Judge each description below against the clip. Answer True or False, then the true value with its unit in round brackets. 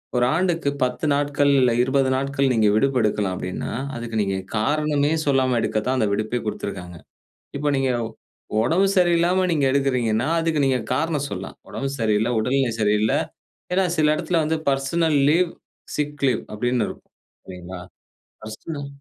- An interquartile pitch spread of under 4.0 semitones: False (5.3 semitones)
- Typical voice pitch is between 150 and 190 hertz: False (135 Hz)